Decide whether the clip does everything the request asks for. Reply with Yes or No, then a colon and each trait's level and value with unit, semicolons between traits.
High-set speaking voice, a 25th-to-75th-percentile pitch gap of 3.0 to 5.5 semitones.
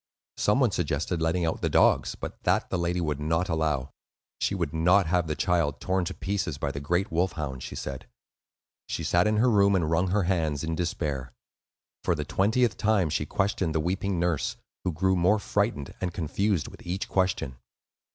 No: very low, 85 Hz; average, 3.5 semitones